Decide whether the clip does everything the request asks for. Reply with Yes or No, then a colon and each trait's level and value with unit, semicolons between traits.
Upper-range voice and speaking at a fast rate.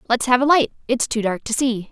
Yes: high, 240 Hz; fast, 280 wpm